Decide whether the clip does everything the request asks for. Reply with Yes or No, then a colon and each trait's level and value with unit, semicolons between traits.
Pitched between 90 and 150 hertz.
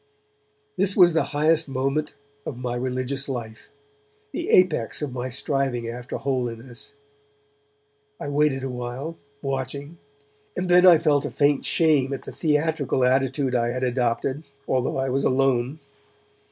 Yes: low, 135 Hz